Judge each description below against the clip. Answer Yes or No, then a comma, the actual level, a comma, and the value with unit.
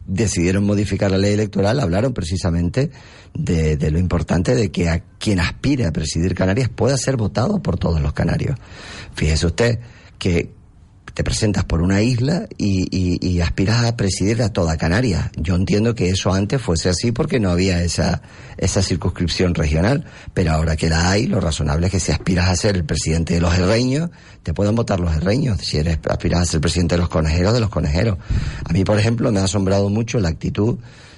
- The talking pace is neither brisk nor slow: No, fast, 195 wpm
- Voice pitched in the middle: No, very low, 95 Hz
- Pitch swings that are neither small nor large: Yes, average, 4.1 semitones